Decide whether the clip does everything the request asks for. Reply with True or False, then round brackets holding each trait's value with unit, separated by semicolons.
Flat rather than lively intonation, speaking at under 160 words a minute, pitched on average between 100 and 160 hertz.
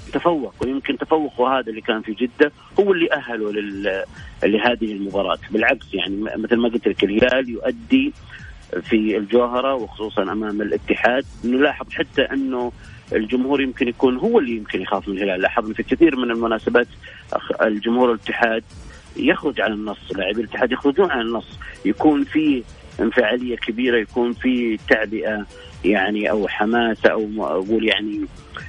False (3.3 semitones; 140 wpm; 120 Hz)